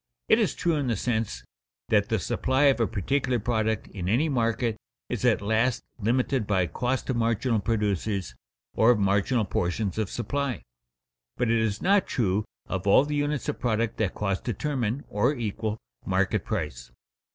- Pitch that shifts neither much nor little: Yes, average, 3.6 semitones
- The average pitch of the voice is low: Yes, low, 110 Hz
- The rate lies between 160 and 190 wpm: Yes, average, 170 wpm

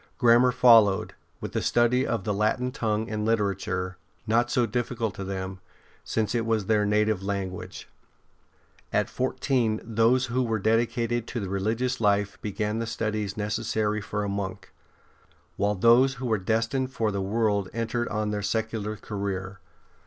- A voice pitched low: Yes, low, 110 Hz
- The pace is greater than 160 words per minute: No, average, 155 wpm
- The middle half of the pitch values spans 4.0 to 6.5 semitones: No, narrow, 2.4 semitones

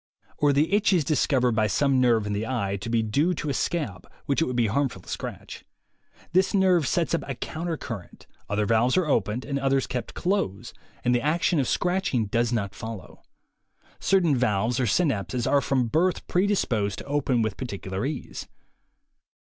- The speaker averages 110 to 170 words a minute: No, average, 185 wpm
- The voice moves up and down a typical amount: No, wide, 5.8 semitones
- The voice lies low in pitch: Yes, low, 130 Hz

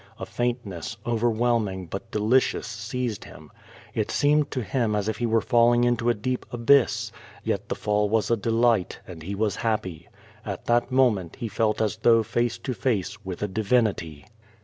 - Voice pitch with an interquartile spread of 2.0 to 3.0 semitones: Yes, average, 2.7 semitones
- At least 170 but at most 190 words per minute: Yes, average, 180 wpm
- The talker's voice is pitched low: Yes, low, 115 Hz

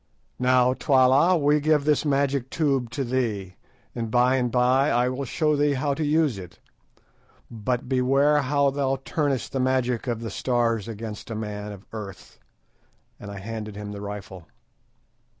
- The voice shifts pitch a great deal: No, average, 3.9 semitones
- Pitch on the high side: No, low, 125 Hz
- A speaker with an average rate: Yes, average, 165 wpm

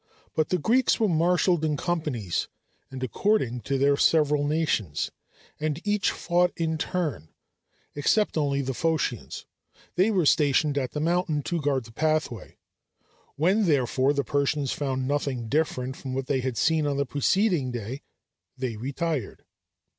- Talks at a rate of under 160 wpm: Yes, average, 150 wpm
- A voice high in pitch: No, medium, 145 Hz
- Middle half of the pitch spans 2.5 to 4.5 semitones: Yes, average, 3.8 semitones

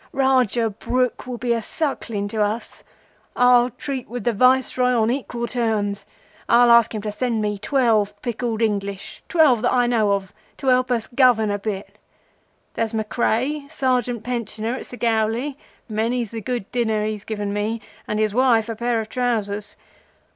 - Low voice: No, high, 230 Hz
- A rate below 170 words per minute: Yes, average, 155 wpm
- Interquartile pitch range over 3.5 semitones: No, average, 2.7 semitones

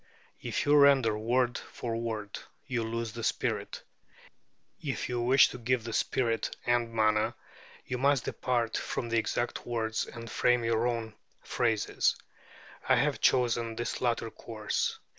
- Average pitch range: No, narrow, 1.4 semitones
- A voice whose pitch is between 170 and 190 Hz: No, low, 115 Hz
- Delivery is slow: No, average, 145 wpm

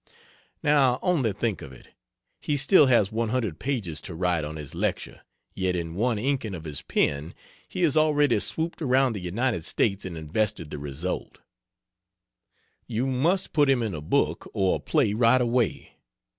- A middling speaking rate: Yes, average, 170 wpm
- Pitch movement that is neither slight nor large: No, wide, 7.3 semitones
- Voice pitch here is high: No, low, 110 Hz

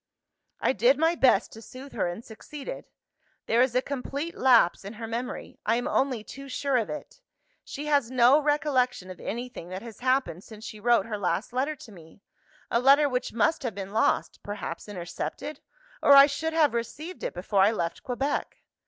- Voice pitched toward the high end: Yes, high, 245 Hz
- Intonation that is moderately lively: Yes, average, 4.8 semitones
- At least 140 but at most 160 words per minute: No, average, 190 wpm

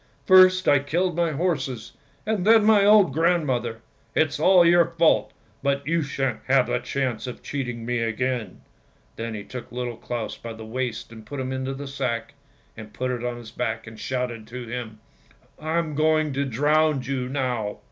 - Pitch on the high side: No, low, 130 Hz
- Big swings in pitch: No, average, 4.6 semitones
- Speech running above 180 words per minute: Yes, average, 190 wpm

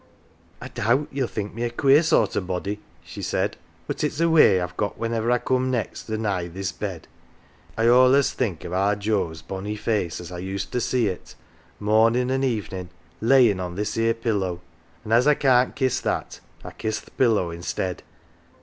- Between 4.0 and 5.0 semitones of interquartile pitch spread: Yes, average, 4.7 semitones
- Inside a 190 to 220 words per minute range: Yes, fast, 205 wpm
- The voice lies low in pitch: Yes, low, 110 Hz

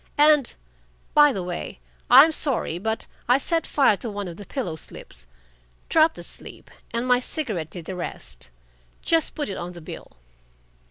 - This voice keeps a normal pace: Yes, average, 165 wpm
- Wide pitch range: Yes, wide, 8.7 semitones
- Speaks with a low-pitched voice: No, high, 225 Hz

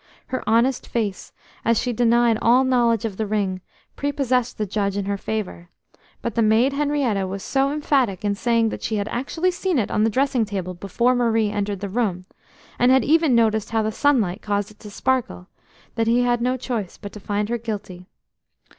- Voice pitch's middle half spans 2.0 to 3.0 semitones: No, average, 3.6 semitones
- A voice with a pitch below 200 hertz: No, high, 225 Hz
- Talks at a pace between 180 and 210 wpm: Yes, average, 200 wpm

